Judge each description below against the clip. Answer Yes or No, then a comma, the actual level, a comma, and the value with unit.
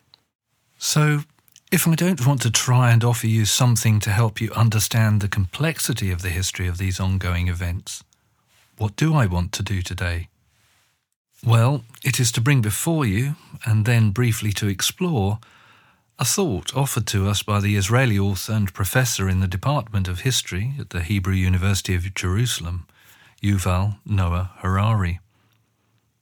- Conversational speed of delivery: Yes, average, 155 wpm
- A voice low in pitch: Yes, low, 110 Hz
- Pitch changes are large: No, average, 4.1 semitones